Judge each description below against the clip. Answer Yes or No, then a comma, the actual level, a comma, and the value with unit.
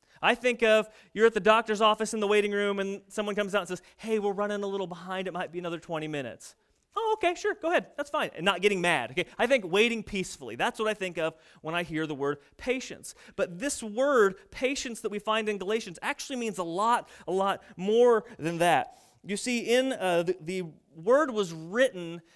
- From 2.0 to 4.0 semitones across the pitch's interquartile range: No, average, 4.5 semitones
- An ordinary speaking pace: No, fast, 225 wpm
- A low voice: No, high, 205 Hz